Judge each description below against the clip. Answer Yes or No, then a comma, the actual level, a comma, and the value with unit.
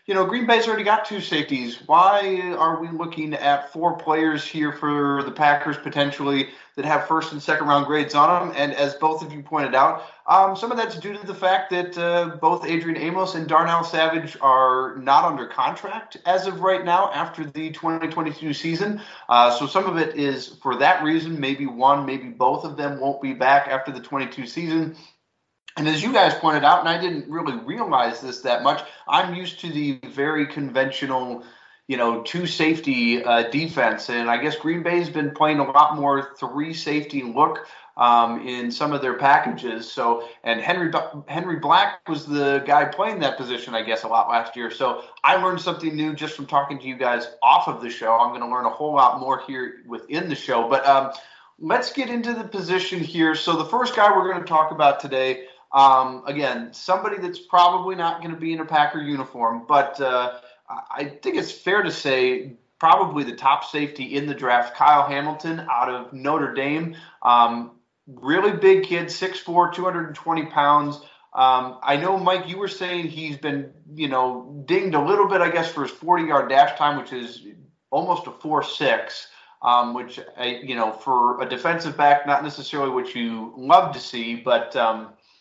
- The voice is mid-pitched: Yes, medium, 150 Hz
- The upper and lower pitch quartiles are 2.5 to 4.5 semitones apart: Yes, average, 4.0 semitones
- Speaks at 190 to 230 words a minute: Yes, average, 195 wpm